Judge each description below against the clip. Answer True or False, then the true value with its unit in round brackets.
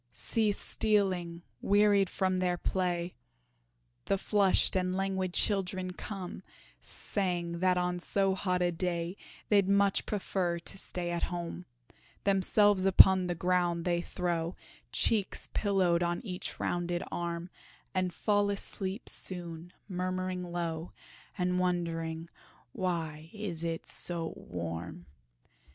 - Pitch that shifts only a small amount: True (2.0 semitones)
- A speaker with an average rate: False (120 wpm)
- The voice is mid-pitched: True (180 Hz)